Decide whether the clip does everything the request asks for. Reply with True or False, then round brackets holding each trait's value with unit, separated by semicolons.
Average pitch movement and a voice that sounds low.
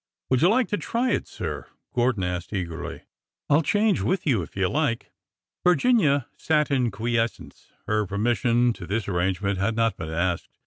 False (7.6 semitones; 115 Hz)